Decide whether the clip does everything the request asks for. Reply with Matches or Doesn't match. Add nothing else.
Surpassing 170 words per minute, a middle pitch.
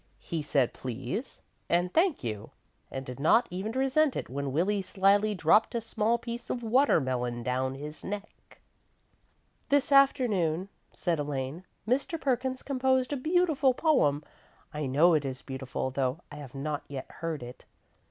Doesn't match